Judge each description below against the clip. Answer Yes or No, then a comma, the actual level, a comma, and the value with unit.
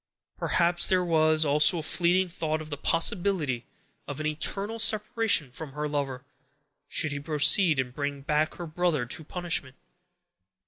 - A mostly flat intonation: No, average, 3.5 semitones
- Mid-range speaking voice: Yes, medium, 155 Hz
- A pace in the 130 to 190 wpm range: Yes, average, 150 wpm